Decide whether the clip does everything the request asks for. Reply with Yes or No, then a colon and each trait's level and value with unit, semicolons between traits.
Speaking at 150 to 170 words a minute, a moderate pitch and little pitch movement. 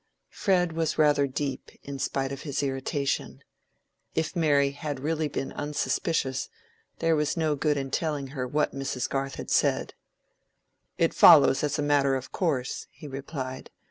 Yes: average, 155 wpm; medium, 145 Hz; narrow, 2.1 semitones